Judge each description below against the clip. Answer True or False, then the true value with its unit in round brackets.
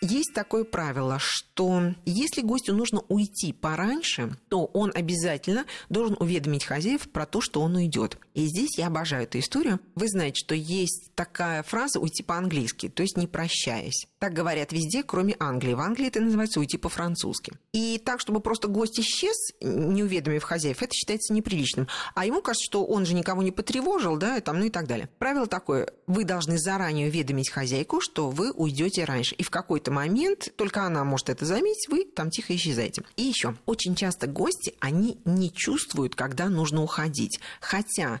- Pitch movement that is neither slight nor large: False (5.8 semitones)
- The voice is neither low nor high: True (180 Hz)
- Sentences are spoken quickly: True (175 wpm)